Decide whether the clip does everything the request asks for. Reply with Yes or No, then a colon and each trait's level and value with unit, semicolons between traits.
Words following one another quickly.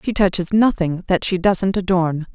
No: average, 180 wpm